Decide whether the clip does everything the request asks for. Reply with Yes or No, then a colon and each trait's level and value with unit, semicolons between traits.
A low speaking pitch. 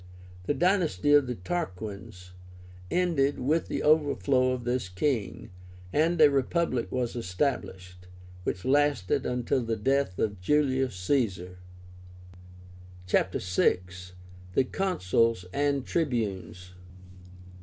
Yes: low, 125 Hz